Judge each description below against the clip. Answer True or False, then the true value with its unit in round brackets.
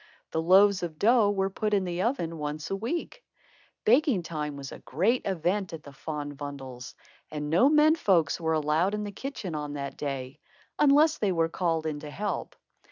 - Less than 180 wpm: False (190 wpm)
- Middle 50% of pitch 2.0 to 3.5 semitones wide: False (5.6 semitones)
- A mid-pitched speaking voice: True (170 Hz)